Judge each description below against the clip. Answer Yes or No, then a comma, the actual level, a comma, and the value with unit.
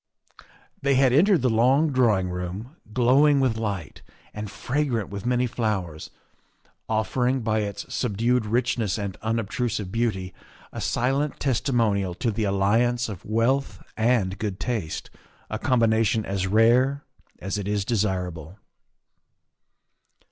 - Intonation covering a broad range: No, average, 3.9 semitones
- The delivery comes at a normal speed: No, slow, 130 wpm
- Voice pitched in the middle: No, low, 110 Hz